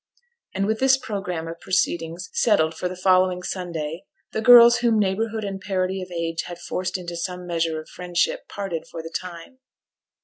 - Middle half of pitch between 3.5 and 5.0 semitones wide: No, average, 3.1 semitones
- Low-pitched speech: No, medium, 185 Hz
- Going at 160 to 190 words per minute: Yes, average, 175 wpm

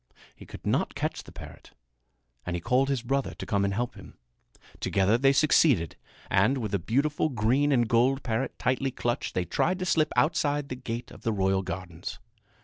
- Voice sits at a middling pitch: No, low, 120 Hz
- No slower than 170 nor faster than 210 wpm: Yes, average, 190 wpm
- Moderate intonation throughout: No, wide, 5.7 semitones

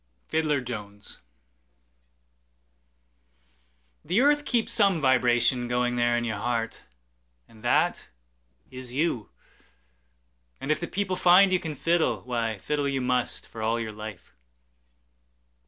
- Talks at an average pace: No, slow, 110 wpm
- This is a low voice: Yes, low, 125 Hz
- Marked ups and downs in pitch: Yes, wide, 6.5 semitones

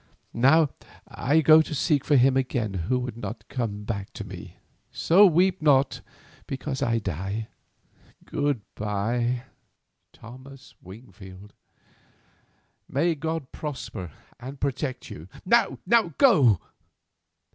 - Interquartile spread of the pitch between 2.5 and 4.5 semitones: No, wide, 5.5 semitones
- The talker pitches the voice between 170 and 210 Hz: No, low, 130 Hz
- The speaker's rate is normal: No, slow, 115 wpm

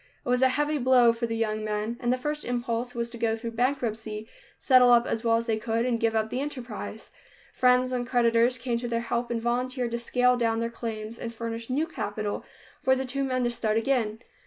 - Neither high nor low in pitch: No, high, 235 Hz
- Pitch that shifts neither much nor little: No, narrow, 1.7 semitones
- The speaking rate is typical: No, fast, 230 wpm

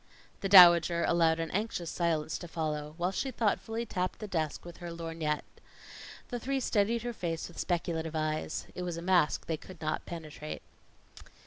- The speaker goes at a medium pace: Yes, average, 175 wpm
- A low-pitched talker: No, medium, 170 Hz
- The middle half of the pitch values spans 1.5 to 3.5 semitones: Yes, average, 2.8 semitones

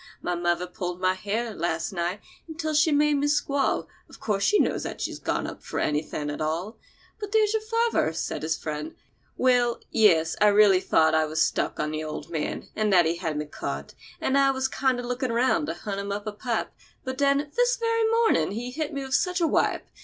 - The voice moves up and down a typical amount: No, wide, 9.0 semitones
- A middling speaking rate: No, fast, 215 wpm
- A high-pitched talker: Yes, high, 215 Hz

